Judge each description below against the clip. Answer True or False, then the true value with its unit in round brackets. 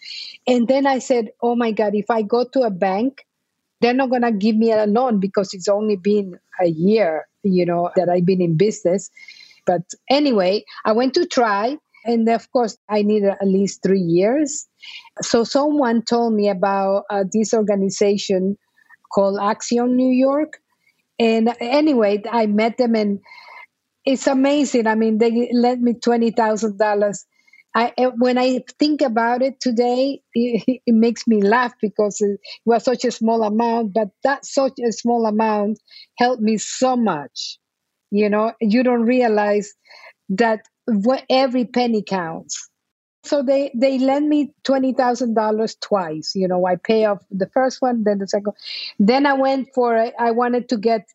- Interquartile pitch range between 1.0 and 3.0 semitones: False (3.6 semitones)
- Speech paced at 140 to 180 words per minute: True (165 wpm)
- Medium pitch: False (230 Hz)